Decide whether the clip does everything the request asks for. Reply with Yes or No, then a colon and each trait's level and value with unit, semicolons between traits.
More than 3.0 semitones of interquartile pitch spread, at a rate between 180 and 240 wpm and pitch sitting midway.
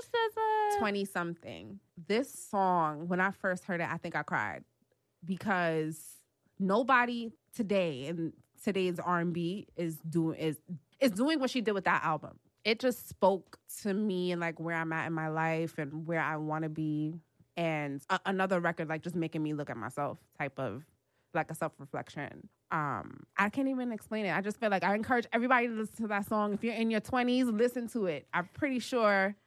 Yes: average, 5.2 semitones; average, 200 wpm; medium, 175 Hz